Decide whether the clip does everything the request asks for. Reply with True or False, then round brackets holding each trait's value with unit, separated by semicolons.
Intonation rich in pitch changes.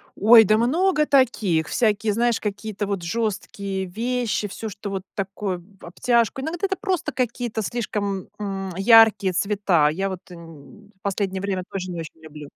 False (3.4 semitones)